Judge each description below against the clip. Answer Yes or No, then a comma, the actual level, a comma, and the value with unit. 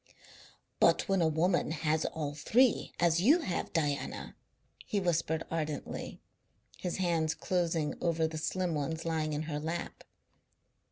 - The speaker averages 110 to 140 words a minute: Yes, slow, 135 wpm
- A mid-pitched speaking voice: Yes, medium, 165 Hz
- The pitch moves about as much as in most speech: No, narrow, 2.0 semitones